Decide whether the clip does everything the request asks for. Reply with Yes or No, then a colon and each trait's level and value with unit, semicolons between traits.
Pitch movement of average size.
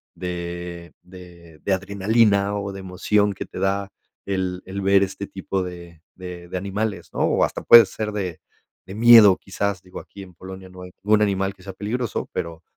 No: narrow, 1.9 semitones